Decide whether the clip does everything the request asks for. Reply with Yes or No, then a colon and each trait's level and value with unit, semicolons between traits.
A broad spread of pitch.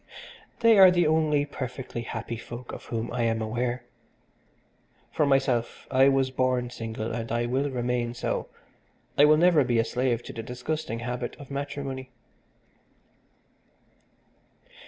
No: average, 3.0 semitones